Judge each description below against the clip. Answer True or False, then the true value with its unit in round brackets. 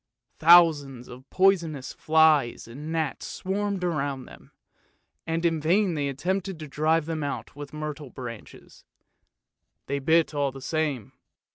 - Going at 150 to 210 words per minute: False (135 wpm)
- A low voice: False (155 Hz)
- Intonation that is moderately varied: True (3.1 semitones)